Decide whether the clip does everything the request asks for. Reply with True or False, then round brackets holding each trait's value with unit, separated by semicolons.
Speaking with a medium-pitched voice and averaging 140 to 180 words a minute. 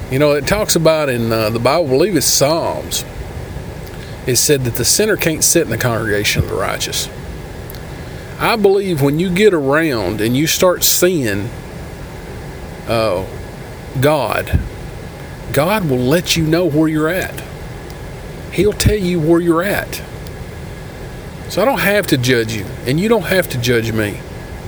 True (150 Hz; 165 wpm)